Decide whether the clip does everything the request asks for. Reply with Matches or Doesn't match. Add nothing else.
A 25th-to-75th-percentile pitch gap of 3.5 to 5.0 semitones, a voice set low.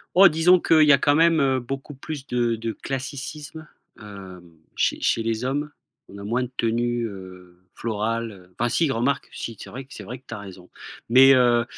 Matches